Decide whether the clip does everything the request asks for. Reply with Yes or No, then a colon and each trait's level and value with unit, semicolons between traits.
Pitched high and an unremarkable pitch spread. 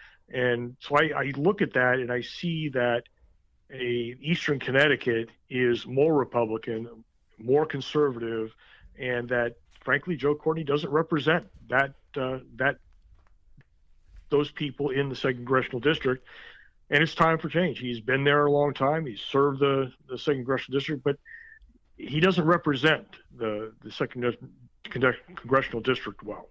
No: low, 135 Hz; average, 3.6 semitones